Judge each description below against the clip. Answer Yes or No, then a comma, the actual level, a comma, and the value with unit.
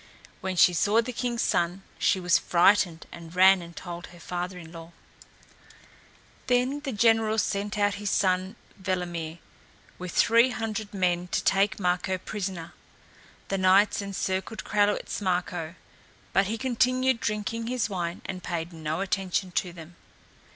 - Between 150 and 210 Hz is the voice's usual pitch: Yes, high, 190 Hz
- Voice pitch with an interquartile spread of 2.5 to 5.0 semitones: Yes, average, 3.1 semitones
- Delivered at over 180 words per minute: No, average, 145 wpm